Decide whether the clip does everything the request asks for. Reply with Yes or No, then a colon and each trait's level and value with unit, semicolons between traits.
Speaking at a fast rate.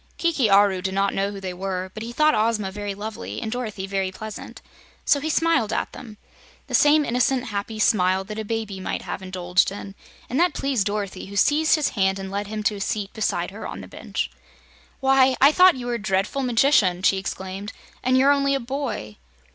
Yes: fast, 210 wpm